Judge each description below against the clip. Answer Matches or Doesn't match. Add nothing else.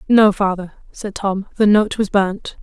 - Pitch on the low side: Doesn't match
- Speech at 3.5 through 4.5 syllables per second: Matches